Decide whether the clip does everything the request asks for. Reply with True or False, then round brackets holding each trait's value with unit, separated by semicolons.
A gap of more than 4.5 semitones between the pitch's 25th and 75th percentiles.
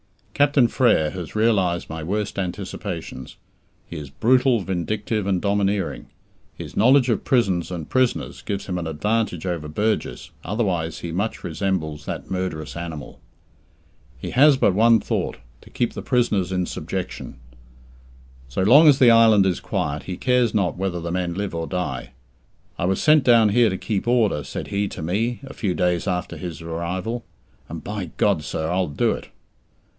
True (4.9 semitones)